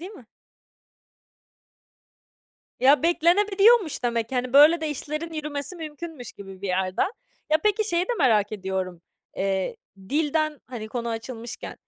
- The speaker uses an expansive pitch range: Yes, wide, 6.6 semitones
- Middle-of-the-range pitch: No, very high, 280 Hz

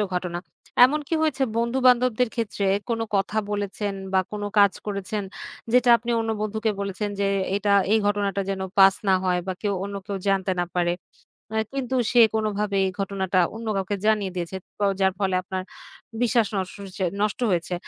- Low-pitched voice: No, high, 205 Hz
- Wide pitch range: No, average, 2.7 semitones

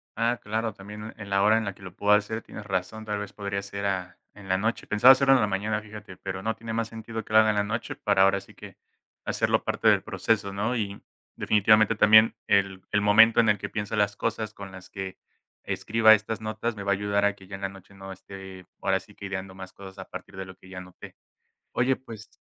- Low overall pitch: Yes, low, 105 Hz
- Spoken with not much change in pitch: Yes, narrow, 2.1 semitones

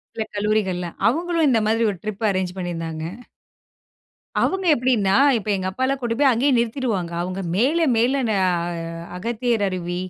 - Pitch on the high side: Yes, high, 220 Hz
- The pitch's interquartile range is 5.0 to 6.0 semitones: Yes, average, 5.3 semitones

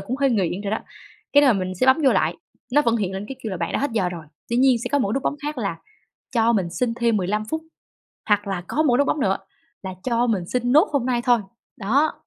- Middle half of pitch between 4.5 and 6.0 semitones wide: Yes, average, 5.2 semitones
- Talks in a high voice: Yes, high, 230 Hz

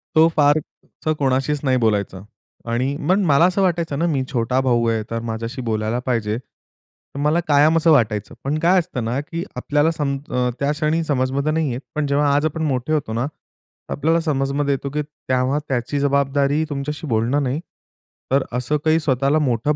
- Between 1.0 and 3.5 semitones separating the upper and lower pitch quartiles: Yes, average, 3.2 semitones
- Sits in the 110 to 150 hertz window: Yes, medium, 140 Hz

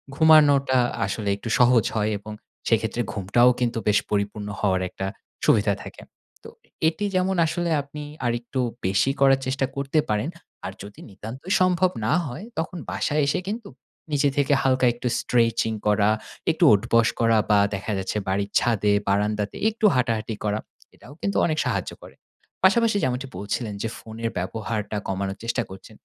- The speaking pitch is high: No, low, 115 Hz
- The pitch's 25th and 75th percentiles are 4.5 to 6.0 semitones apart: Yes, average, 5.2 semitones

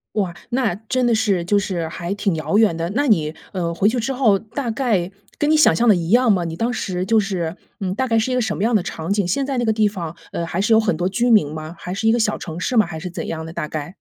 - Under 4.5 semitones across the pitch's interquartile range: No, average, 4.8 semitones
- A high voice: Yes, high, 200 Hz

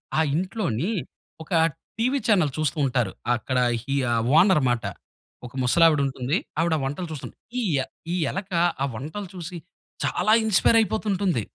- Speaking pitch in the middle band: Yes, medium, 165 Hz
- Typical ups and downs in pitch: No, wide, 6.3 semitones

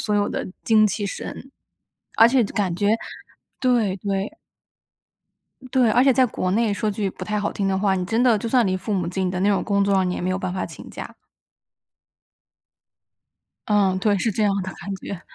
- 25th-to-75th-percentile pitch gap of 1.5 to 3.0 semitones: Yes, average, 2.7 semitones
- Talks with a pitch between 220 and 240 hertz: No, high, 200 Hz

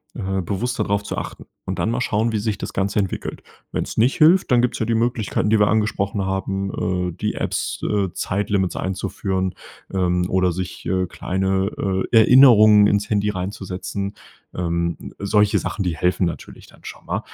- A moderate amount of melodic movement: No, narrow, 2.3 semitones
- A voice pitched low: Yes, low, 100 Hz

